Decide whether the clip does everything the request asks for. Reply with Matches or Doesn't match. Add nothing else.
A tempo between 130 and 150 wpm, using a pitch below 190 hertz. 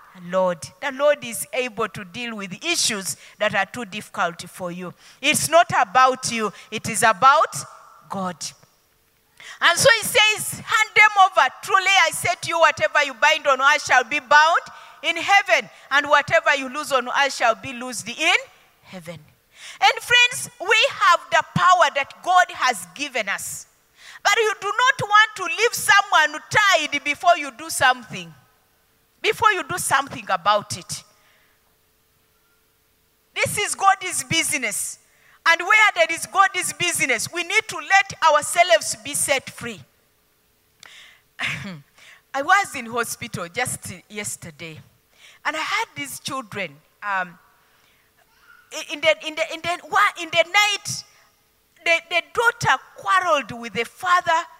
Doesn't match